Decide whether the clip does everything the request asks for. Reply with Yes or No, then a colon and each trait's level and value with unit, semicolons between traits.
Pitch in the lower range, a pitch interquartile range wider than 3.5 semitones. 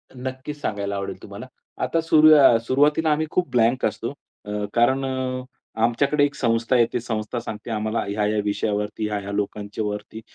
Yes: low, 115 Hz; average, 4.1 semitones